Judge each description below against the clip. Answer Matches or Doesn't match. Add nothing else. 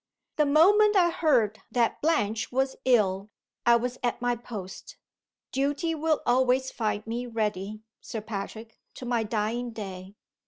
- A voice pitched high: Matches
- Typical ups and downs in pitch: Matches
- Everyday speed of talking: Matches